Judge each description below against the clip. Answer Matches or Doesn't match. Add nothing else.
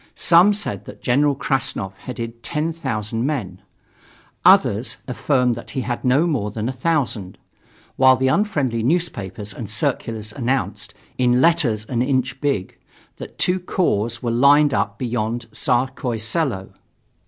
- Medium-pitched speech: Doesn't match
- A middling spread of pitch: Matches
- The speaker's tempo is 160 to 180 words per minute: Doesn't match